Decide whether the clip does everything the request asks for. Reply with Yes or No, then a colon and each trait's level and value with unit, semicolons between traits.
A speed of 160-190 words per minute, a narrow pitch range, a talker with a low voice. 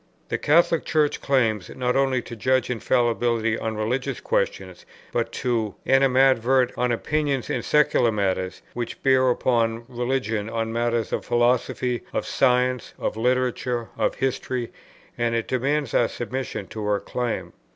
No: average, 140 wpm; narrow, 2.3 semitones; low, 125 Hz